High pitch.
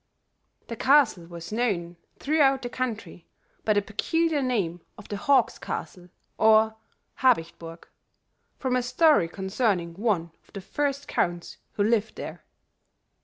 Yes: high, 220 Hz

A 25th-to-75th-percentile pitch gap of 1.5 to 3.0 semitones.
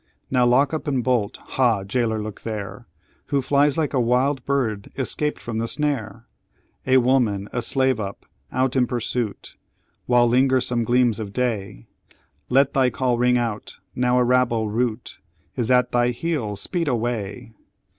Yes: narrow, 2.6 semitones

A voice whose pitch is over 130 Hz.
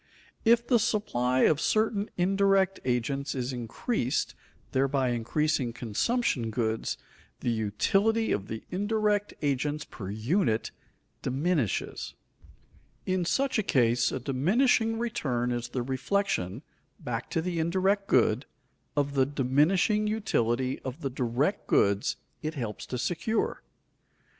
Yes: medium, 140 Hz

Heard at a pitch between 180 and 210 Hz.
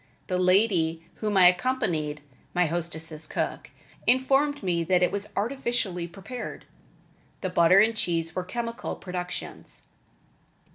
Yes: medium, 185 Hz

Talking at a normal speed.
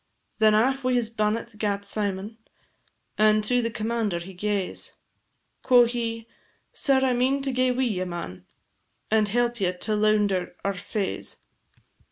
Yes: average, 150 wpm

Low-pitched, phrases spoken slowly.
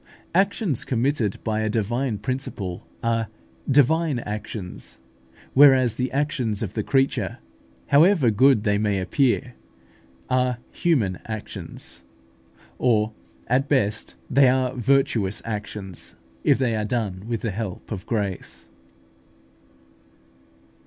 Yes: low, 115 Hz; slow, 110 wpm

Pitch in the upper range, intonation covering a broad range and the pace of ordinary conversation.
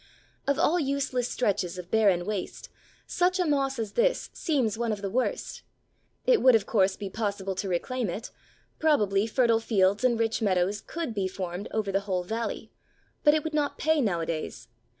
Yes: high, 220 Hz; wide, 5.7 semitones; average, 180 wpm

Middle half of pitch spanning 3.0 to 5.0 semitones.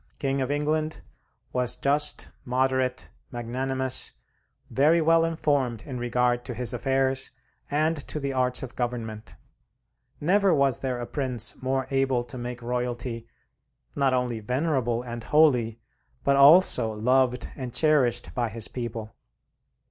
No: narrow, 2.5 semitones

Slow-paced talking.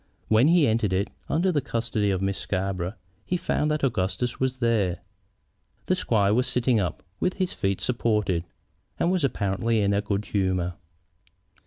No: average, 165 wpm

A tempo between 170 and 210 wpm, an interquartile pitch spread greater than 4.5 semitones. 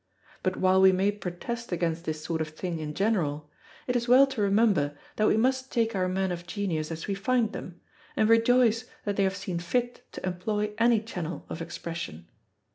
Yes: average, 200 wpm; average, 4.9 semitones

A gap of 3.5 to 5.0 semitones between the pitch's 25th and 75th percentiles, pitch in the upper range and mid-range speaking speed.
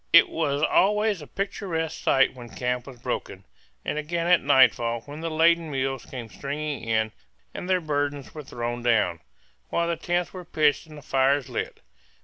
No: average, 4.6 semitones; medium, 145 Hz; average, 175 wpm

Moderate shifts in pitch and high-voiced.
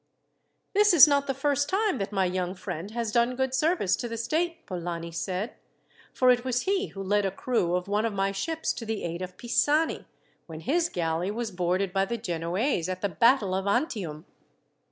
No: wide, 6.4 semitones; high, 210 Hz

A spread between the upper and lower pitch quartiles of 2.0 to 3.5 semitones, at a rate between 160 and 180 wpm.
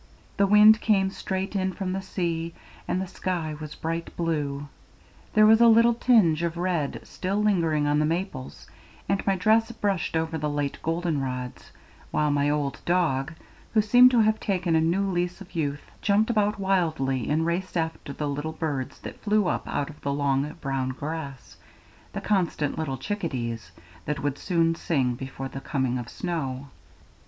No: average, 5.1 semitones; average, 175 wpm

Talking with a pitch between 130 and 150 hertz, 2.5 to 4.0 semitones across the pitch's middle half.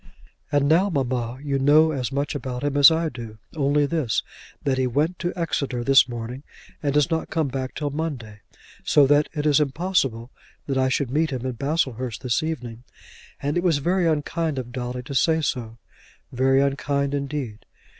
Yes: medium, 140 Hz; average, 3.2 semitones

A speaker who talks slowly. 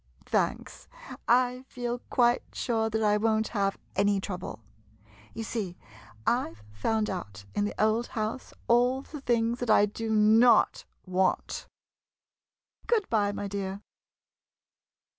Yes: slow, 130 wpm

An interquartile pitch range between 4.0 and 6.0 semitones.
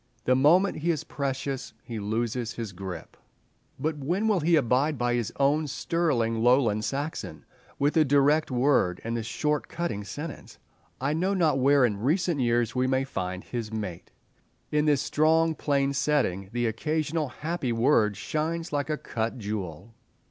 Yes: average, 5.0 semitones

